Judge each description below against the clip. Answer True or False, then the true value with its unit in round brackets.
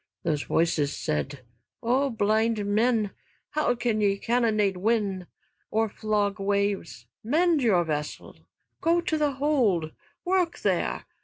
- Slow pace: True (125 wpm)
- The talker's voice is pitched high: True (215 Hz)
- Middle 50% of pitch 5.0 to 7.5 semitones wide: False (4.2 semitones)